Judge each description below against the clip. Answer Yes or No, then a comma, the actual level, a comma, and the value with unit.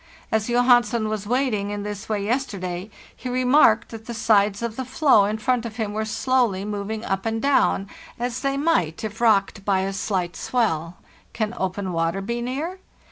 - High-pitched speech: Yes, high, 220 Hz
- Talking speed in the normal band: Yes, average, 190 wpm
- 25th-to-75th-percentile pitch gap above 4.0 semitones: No, average, 3.5 semitones